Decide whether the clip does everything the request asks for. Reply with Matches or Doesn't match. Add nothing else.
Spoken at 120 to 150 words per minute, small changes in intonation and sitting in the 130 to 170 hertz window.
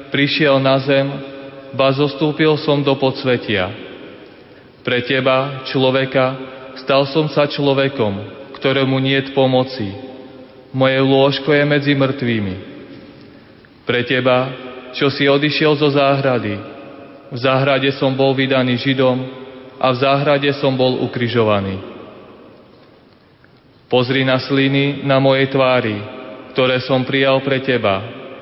Doesn't match